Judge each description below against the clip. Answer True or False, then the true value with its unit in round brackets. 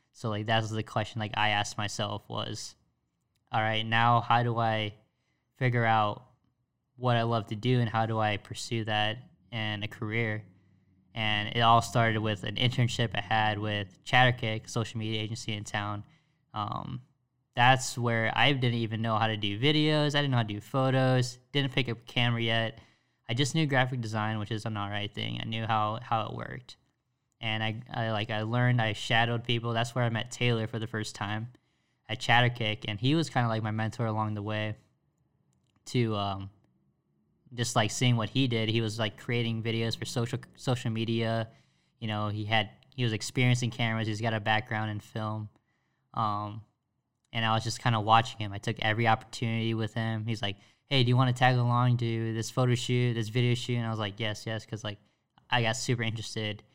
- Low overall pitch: True (115 Hz)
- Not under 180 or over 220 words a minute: True (205 wpm)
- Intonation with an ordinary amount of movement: False (2.2 semitones)